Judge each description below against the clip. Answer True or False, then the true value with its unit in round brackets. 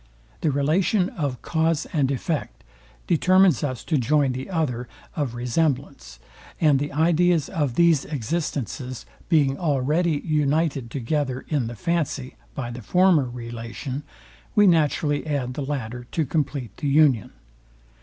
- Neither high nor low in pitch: True (145 Hz)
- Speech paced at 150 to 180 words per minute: False (135 wpm)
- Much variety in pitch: False (4.0 semitones)